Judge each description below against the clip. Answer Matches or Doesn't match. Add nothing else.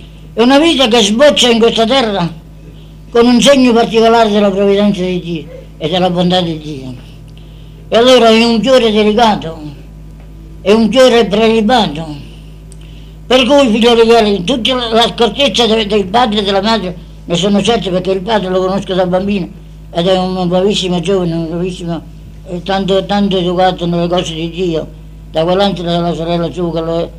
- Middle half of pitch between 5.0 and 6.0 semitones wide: Matches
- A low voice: Doesn't match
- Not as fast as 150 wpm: Doesn't match